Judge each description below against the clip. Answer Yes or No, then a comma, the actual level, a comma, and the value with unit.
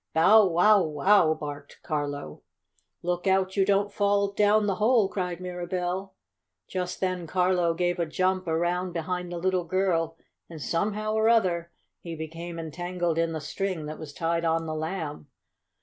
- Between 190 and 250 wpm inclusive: No, average, 160 wpm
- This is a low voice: No, medium, 180 Hz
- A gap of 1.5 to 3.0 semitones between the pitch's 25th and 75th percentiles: Yes, average, 2.7 semitones